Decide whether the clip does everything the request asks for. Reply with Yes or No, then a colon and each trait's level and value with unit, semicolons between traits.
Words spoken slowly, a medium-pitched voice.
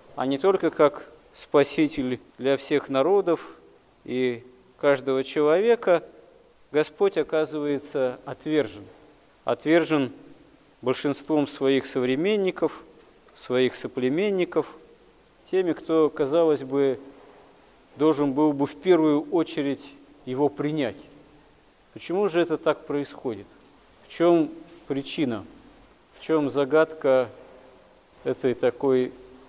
Yes: slow, 90 wpm; medium, 150 Hz